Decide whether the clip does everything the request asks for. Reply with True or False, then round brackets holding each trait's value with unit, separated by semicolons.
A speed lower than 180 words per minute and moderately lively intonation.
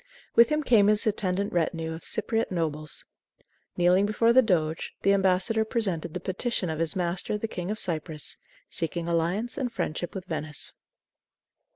True (160 wpm; 4.5 semitones)